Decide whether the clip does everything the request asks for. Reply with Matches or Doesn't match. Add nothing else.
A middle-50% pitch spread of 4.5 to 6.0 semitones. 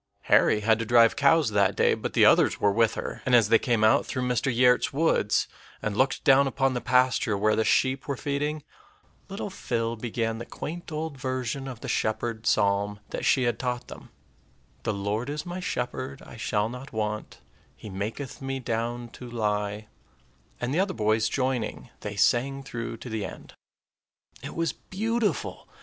Doesn't match